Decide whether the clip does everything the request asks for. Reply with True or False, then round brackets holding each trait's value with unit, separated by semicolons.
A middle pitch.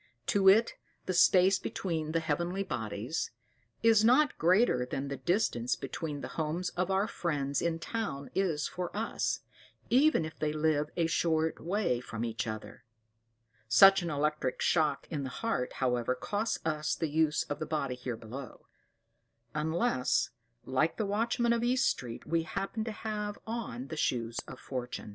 True (160 Hz)